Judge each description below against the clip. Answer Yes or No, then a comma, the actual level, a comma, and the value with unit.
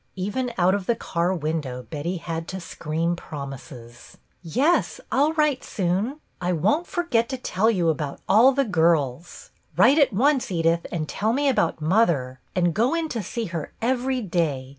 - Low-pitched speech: No, medium, 180 Hz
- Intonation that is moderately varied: No, wide, 7.2 semitones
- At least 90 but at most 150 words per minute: No, average, 175 wpm